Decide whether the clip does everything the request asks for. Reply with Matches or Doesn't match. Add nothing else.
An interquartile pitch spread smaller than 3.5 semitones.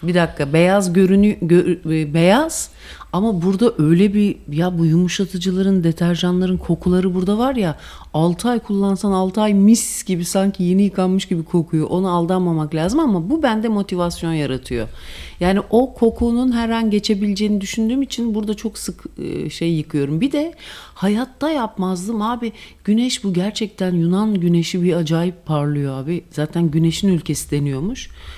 Doesn't match